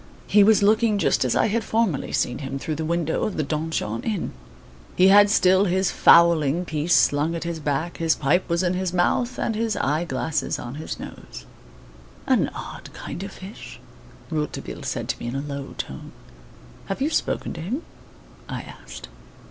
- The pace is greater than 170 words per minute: Yes, average, 185 wpm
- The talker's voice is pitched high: No, medium, 170 Hz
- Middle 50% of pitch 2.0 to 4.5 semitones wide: No, average, 4.9 semitones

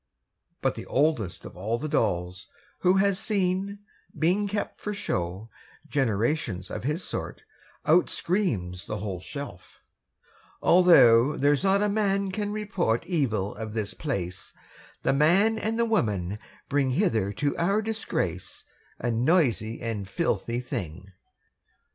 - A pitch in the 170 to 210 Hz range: No, low, 135 Hz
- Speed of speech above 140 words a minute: No, slow, 135 wpm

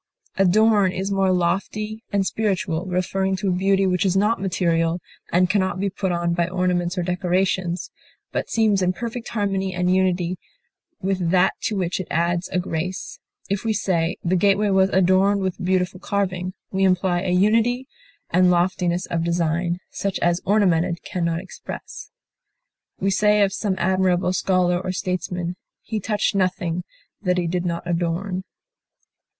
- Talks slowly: No, average, 160 wpm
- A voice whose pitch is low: No, medium, 185 Hz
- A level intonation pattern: Yes, narrow, 1.7 semitones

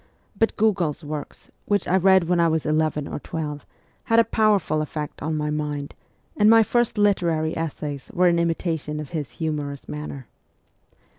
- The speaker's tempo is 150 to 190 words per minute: Yes, average, 165 wpm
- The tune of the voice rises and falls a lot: No, average, 3.9 semitones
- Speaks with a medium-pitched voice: Yes, medium, 160 Hz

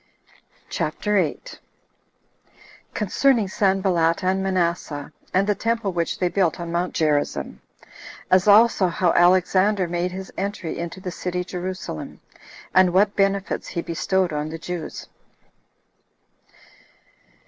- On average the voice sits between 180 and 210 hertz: Yes, medium, 185 Hz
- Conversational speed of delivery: No, slow, 115 wpm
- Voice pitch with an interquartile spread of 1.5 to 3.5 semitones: Yes, narrow, 2.4 semitones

